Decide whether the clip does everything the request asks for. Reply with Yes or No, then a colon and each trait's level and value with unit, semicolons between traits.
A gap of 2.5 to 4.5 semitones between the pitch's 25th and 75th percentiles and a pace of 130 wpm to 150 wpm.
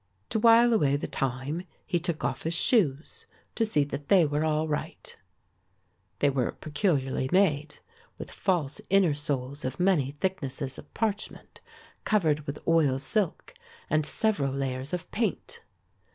No: wide, 5.4 semitones; average, 145 wpm